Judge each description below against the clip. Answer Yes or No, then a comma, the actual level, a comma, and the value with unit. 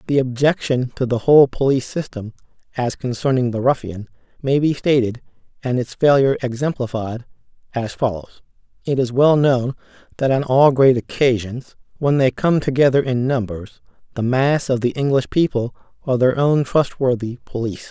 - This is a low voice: Yes, low, 130 Hz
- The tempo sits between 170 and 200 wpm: No, average, 155 wpm